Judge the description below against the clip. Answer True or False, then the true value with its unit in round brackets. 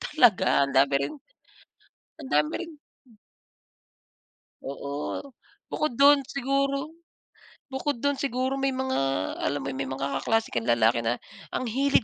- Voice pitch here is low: False (245 Hz)